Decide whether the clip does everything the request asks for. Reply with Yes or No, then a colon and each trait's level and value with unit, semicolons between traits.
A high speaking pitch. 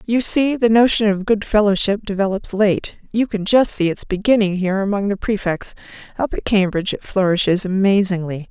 Yes: high, 200 Hz